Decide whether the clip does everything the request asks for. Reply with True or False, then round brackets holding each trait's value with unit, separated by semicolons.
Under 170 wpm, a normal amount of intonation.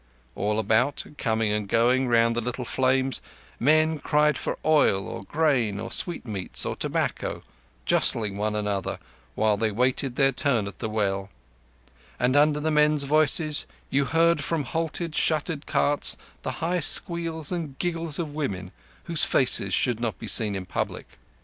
False (155 wpm; 6.0 semitones)